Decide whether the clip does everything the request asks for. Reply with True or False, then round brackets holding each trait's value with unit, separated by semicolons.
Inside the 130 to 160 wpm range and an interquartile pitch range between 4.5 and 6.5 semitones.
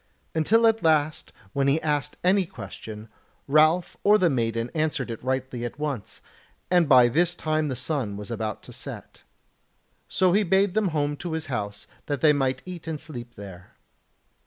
False (175 wpm; 5.6 semitones)